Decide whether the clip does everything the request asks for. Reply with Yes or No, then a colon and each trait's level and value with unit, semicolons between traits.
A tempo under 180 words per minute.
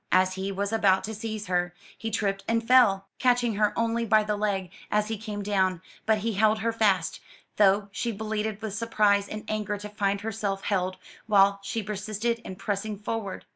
No: average, 190 wpm